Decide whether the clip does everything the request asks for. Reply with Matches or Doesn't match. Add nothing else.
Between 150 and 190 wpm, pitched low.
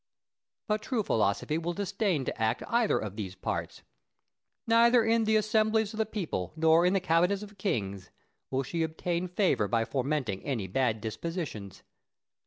Doesn't match